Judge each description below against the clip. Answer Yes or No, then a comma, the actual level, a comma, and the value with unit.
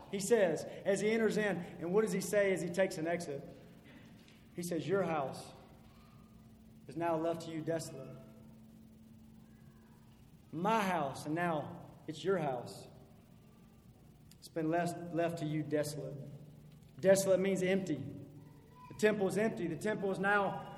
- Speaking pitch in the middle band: Yes, medium, 170 Hz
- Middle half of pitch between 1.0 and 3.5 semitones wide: No, average, 4.0 semitones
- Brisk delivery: No, average, 145 wpm